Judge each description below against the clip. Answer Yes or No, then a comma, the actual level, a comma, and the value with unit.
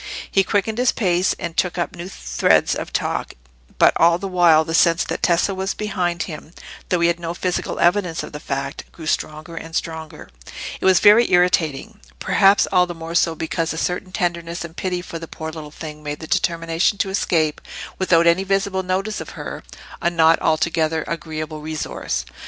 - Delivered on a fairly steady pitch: Yes, narrow, 2.3 semitones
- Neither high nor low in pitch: Yes, medium, 170 Hz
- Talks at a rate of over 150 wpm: Yes, average, 185 wpm